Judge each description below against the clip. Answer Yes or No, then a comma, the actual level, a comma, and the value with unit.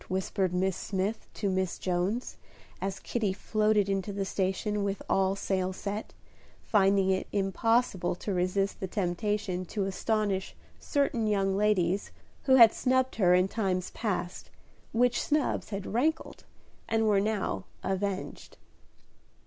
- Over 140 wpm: No, slow, 135 wpm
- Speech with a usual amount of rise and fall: No, narrow, 2.3 semitones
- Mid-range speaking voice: No, high, 195 Hz